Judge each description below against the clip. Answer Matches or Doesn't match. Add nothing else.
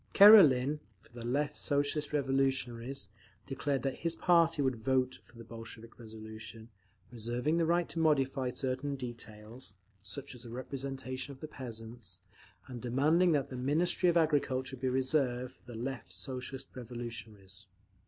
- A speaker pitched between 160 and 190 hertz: Doesn't match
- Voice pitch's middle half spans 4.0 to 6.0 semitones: Doesn't match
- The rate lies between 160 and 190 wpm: Doesn't match